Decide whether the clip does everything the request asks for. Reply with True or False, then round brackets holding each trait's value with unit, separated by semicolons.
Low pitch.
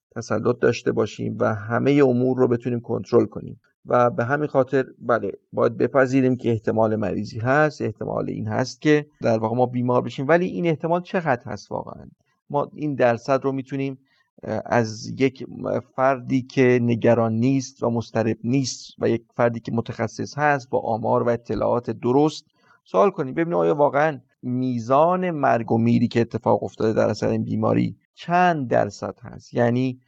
True (125 Hz)